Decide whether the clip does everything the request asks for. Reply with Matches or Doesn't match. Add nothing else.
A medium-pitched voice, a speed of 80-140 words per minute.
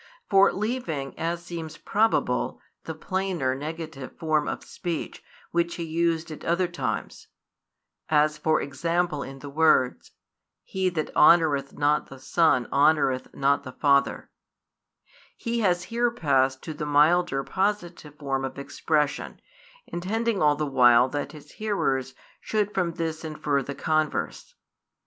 Matches